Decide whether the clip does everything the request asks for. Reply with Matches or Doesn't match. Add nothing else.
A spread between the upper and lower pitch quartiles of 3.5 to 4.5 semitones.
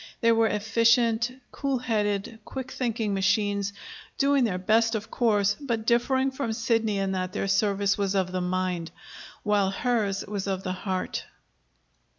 Doesn't match